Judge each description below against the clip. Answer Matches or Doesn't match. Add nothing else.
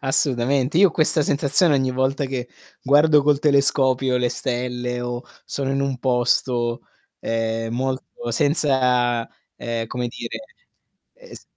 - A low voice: Matches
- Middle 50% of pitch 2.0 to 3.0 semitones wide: Matches